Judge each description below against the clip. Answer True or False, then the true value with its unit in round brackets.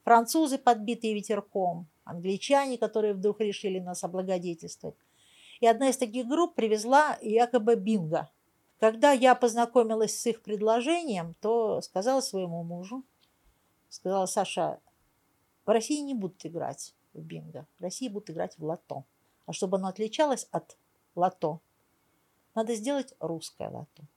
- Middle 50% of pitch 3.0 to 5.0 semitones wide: False (5.4 semitones)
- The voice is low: False (215 Hz)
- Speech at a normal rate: True (130 wpm)